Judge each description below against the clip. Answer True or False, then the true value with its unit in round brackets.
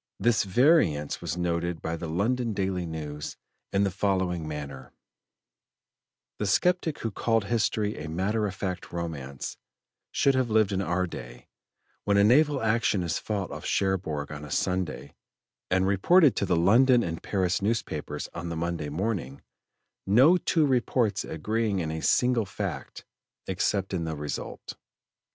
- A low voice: True (95 Hz)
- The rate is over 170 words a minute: False (150 wpm)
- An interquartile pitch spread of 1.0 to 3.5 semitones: False (5.3 semitones)